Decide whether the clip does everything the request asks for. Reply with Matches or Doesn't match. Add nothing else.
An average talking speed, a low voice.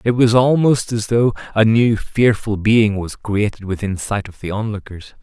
Matches